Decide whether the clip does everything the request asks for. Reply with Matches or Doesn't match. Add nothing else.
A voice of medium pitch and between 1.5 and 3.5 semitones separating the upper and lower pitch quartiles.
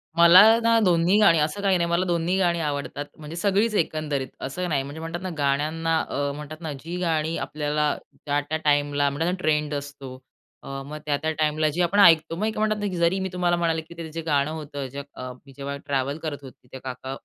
Matches